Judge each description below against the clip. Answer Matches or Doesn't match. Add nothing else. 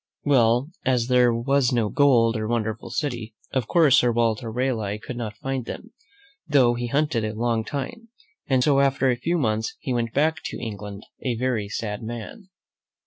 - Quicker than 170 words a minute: Matches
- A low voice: Matches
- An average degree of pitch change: Matches